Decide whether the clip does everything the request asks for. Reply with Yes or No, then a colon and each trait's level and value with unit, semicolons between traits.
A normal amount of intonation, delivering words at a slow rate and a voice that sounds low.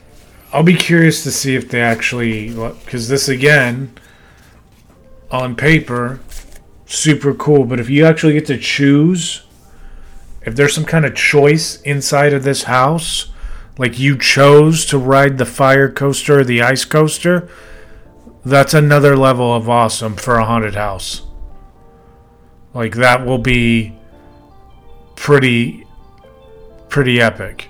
Yes: average, 4.0 semitones; slow, 130 wpm; low, 130 Hz